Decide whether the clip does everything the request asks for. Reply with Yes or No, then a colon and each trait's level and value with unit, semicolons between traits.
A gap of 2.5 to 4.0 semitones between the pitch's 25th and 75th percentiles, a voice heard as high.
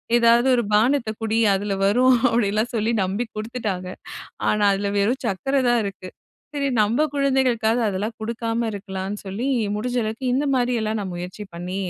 Yes: average, 3.3 semitones; high, 220 Hz